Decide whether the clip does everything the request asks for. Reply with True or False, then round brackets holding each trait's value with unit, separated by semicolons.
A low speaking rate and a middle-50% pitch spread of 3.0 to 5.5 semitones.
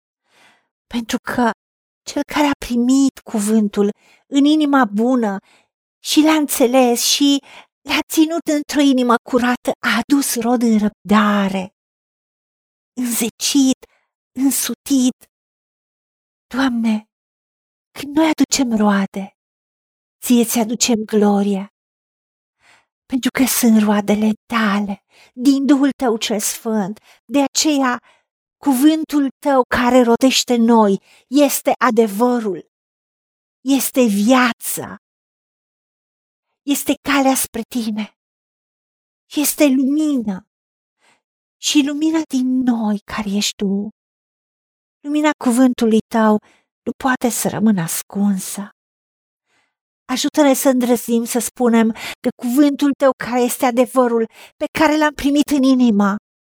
True (100 wpm; 4.0 semitones)